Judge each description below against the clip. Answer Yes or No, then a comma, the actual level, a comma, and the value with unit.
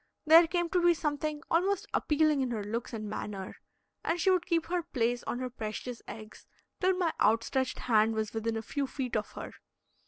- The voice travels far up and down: Yes, wide, 6.8 semitones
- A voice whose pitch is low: No, very high, 260 Hz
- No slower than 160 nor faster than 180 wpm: No, average, 195 wpm